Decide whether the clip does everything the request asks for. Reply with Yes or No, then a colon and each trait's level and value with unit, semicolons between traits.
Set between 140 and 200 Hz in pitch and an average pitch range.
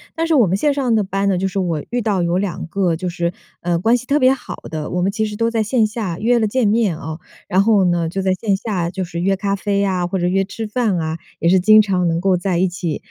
Yes: high, 195 Hz; average, 3.6 semitones